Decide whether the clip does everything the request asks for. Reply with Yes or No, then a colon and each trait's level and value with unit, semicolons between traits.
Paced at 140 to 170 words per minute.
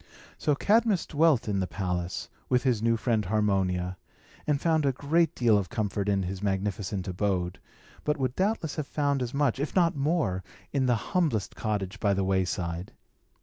No: average, 180 wpm